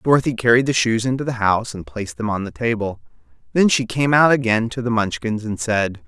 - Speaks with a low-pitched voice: Yes, low, 115 Hz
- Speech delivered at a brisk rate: Yes, fast, 225 wpm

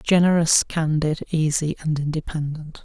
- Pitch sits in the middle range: Yes, medium, 155 Hz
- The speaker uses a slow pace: Yes, slow, 105 wpm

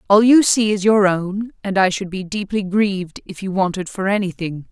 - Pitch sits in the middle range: No, high, 195 Hz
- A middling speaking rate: No, fast, 230 wpm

